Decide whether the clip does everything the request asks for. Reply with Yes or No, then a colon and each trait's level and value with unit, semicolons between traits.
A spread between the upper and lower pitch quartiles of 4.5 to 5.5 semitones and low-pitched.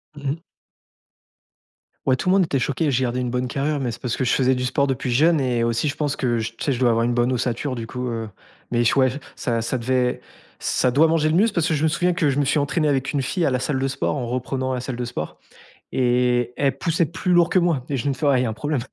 No: average, 3.1 semitones; low, 130 Hz